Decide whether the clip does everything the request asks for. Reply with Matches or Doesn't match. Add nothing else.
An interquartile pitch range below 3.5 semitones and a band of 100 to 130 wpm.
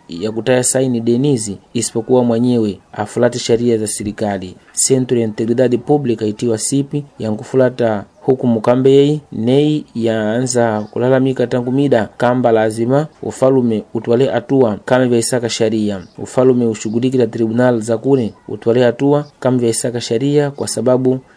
Matches